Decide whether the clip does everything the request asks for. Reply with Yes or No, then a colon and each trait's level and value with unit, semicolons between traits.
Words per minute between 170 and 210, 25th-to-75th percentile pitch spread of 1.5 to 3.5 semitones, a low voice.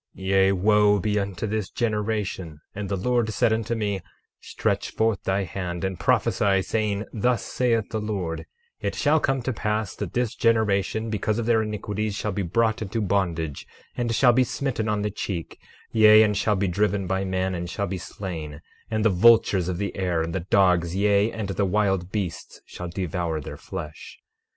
Yes: average, 190 wpm; average, 2.8 semitones; low, 100 Hz